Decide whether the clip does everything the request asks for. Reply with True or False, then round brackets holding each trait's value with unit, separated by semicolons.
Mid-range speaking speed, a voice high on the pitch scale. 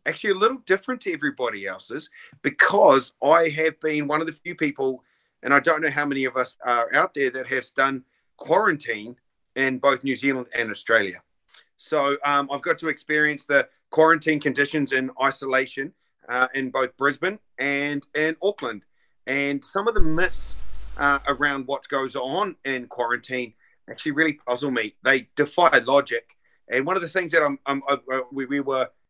False (180 wpm; 140 Hz)